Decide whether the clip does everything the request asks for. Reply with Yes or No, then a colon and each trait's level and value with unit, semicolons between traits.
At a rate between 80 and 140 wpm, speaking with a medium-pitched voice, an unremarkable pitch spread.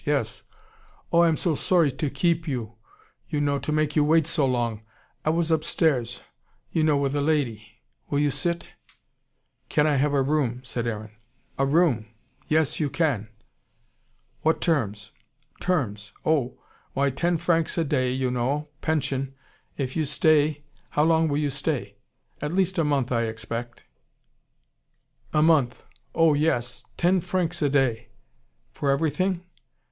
No: average, 155 wpm; medium, 145 Hz; average, 4.0 semitones